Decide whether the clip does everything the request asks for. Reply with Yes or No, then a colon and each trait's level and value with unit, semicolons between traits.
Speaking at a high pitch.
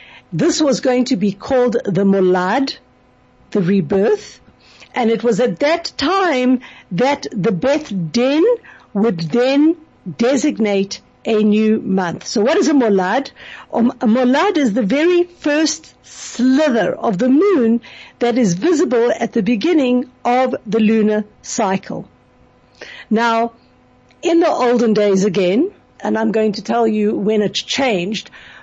Yes: high, 235 Hz